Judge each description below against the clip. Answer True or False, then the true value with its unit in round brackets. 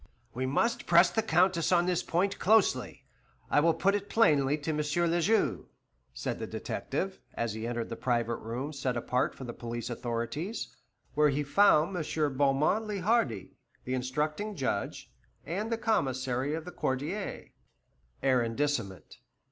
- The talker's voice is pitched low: False (150 Hz)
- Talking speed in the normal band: True (155 wpm)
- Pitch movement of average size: False (6.3 semitones)